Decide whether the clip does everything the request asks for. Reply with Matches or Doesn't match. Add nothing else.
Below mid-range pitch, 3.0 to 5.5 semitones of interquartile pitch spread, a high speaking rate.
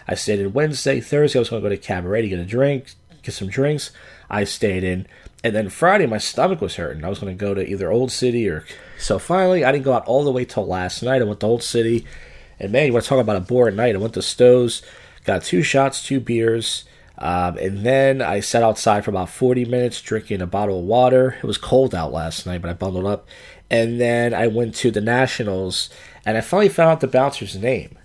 Matches